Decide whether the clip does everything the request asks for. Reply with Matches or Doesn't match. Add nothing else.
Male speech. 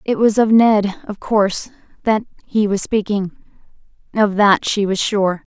Doesn't match